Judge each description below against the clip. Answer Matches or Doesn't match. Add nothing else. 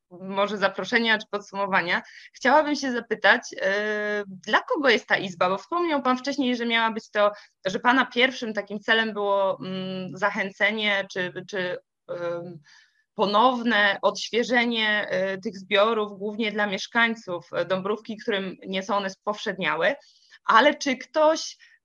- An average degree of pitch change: Matches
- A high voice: Matches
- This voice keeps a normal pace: Matches